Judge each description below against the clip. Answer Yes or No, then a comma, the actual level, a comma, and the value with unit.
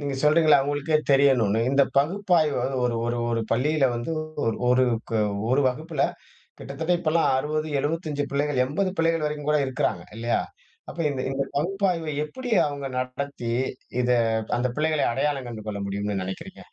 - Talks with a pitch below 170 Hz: Yes, medium, 140 Hz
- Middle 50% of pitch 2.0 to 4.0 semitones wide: Yes, average, 3.5 semitones